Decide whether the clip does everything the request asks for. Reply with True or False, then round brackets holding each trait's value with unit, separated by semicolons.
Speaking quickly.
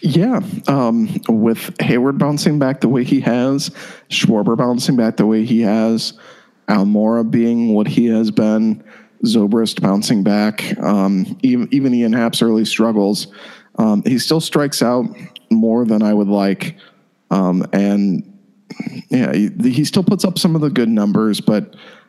False (155 wpm)